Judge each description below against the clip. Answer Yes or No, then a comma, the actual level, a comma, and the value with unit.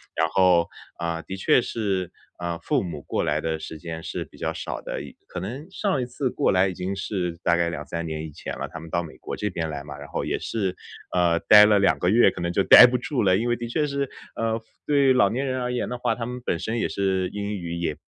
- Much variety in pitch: Yes, wide, 6.0 semitones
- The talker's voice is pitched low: Yes, very low, 95 Hz